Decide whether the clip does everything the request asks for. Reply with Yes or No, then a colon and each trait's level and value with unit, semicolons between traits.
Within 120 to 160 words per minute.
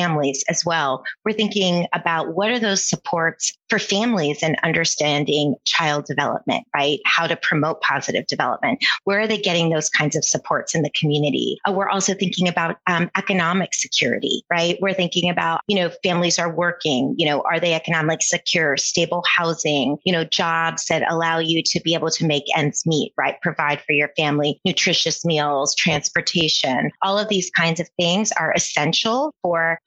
No: average, 175 wpm